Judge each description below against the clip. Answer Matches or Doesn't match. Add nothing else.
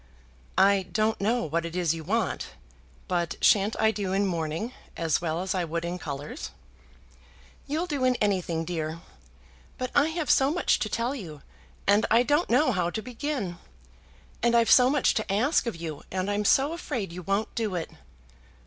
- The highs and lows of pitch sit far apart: Matches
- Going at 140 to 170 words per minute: Doesn't match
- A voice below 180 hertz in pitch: Doesn't match